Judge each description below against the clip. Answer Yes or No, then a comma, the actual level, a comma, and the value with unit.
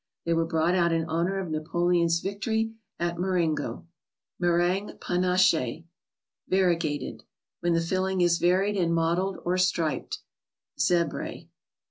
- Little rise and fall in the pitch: Yes, narrow, 1.9 semitones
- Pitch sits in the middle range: Yes, medium, 175 Hz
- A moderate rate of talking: No, slow, 125 wpm